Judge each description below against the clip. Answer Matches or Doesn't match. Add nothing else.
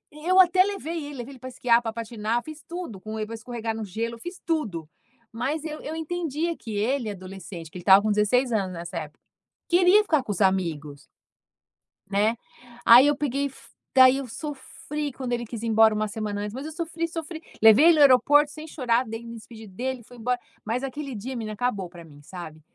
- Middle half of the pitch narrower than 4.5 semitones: Doesn't match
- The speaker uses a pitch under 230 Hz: Doesn't match